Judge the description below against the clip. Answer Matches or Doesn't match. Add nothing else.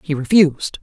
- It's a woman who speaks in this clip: Matches